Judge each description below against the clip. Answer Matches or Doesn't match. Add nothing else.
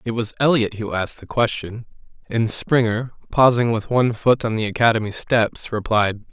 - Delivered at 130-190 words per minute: Matches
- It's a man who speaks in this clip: Matches